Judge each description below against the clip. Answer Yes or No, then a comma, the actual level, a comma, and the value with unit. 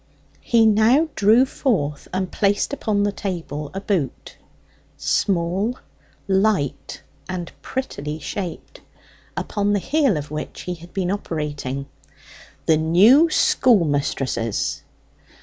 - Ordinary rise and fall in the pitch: No, wide, 6.0 semitones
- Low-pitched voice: No, high, 190 Hz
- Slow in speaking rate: Yes, slow, 110 wpm